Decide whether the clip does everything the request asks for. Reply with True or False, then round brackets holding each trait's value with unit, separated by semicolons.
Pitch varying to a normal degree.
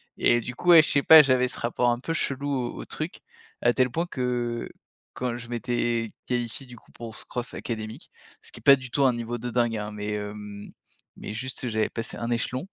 False (1.9 semitones)